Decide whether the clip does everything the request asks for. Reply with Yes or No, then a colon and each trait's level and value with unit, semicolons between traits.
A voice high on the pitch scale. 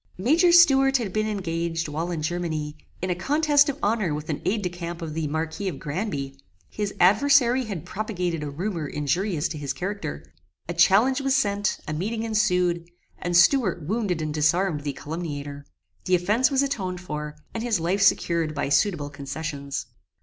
No: medium, 175 Hz